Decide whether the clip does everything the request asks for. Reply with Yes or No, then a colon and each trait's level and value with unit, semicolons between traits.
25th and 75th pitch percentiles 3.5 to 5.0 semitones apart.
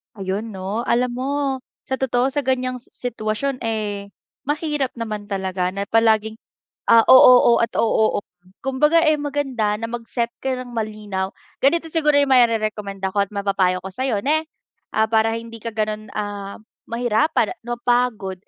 Yes: average, 3.8 semitones